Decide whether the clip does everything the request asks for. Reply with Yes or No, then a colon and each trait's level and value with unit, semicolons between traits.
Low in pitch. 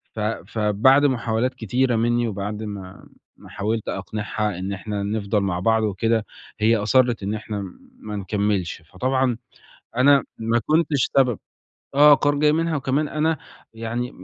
Yes: low, 110 Hz